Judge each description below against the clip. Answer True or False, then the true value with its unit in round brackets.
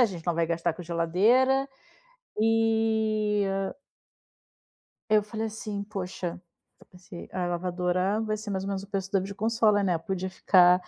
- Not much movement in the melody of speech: False (3.3 semitones)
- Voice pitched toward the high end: True (195 Hz)